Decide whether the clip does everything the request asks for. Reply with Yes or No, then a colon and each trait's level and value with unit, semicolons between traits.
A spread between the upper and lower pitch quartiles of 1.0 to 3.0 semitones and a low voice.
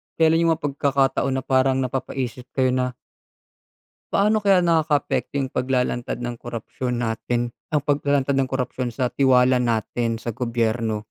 Yes: narrow, 2.5 semitones; low, 130 Hz